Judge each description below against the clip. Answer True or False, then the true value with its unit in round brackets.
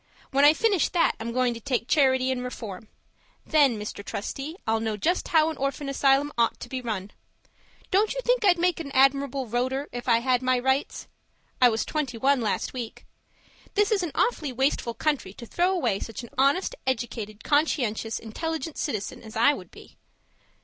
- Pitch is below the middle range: False (260 Hz)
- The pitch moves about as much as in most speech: True (4.6 semitones)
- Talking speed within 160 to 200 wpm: True (185 wpm)